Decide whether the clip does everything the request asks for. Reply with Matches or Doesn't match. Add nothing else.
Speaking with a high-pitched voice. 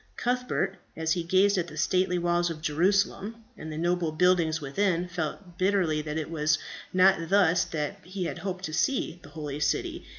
Doesn't match